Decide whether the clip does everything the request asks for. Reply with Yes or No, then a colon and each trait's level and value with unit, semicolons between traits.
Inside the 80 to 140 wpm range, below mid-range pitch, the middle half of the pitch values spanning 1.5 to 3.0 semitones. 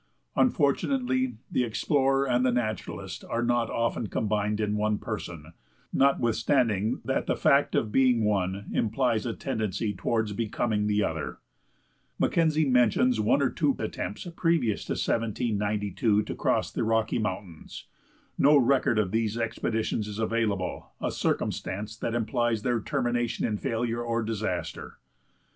Yes: slow, 135 wpm; low, 115 Hz; average, 2.7 semitones